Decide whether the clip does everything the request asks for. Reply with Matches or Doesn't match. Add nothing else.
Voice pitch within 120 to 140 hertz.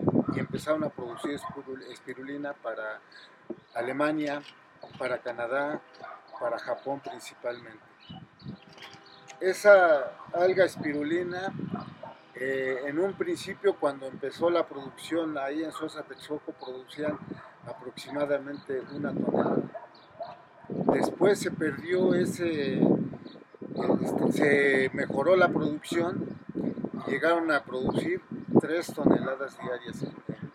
Doesn't match